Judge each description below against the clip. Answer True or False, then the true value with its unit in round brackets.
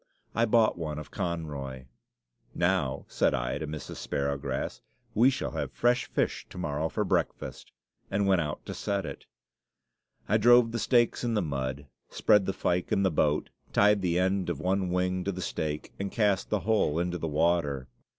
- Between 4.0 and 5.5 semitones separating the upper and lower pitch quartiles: True (5.1 semitones)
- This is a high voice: False (90 Hz)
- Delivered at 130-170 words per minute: False (180 wpm)